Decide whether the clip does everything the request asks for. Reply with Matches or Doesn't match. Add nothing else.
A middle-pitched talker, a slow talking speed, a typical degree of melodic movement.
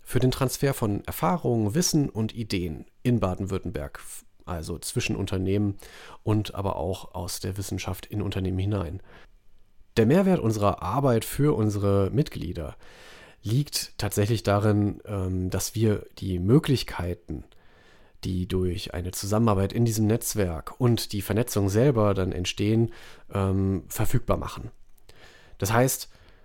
Doesn't match